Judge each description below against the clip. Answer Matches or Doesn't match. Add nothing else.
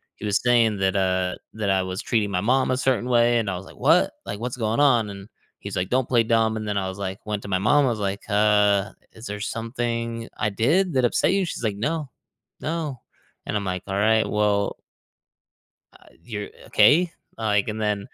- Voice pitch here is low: Matches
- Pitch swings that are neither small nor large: Matches